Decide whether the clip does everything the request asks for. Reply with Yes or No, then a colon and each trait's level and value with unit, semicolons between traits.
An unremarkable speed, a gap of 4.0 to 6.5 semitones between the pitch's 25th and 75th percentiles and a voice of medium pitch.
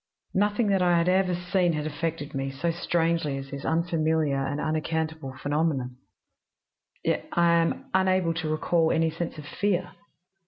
No: average, 155 wpm; average, 2.7 semitones; medium, 165 Hz